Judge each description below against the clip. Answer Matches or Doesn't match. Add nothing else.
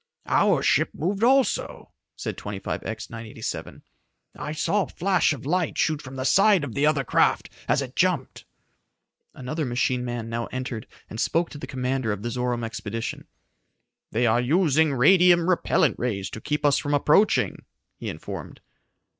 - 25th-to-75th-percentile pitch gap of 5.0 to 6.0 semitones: Matches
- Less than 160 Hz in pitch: Matches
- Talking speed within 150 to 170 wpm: Matches